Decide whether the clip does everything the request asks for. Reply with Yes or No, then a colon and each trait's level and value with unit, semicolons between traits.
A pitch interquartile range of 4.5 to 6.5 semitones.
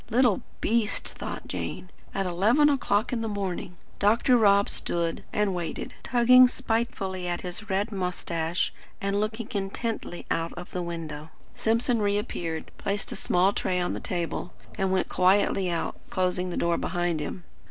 No: average, 3.6 semitones